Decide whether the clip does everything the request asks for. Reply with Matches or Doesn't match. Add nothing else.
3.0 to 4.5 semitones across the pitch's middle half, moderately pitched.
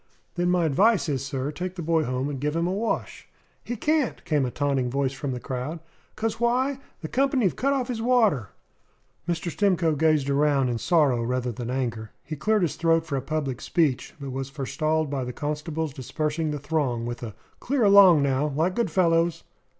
Doesn't match